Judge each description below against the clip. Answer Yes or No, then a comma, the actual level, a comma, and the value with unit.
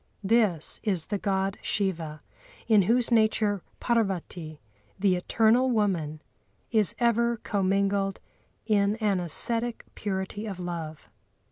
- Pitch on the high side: Yes, high, 200 Hz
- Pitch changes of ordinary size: Yes, average, 3.5 semitones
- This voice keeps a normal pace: No, slow, 110 wpm